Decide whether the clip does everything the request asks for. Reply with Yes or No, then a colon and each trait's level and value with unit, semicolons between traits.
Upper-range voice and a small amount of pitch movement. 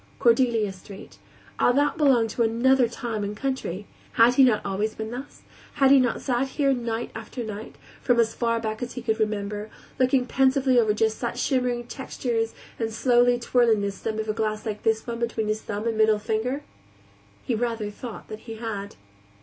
Yes: high, 230 Hz; narrow, 2.3 semitones